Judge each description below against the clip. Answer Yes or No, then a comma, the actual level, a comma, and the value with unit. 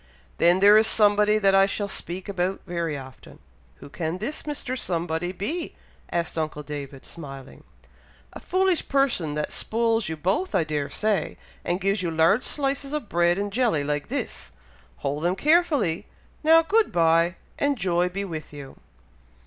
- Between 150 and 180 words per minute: Yes, average, 165 wpm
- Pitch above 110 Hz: Yes, medium, 185 Hz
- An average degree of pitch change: No, wide, 5.7 semitones